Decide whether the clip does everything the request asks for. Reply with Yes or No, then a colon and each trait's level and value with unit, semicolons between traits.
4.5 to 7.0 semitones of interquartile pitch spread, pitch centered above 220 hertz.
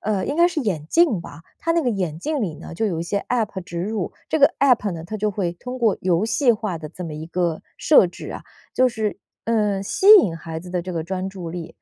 No: average, 5.2 semitones; high, 195 Hz